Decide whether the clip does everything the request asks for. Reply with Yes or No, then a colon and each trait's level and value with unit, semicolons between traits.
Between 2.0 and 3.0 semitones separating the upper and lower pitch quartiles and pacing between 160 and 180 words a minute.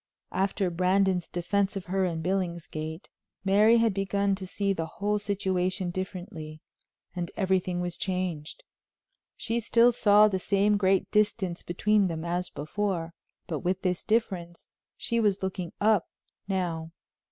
No: narrow, 2.5 semitones; average, 140 wpm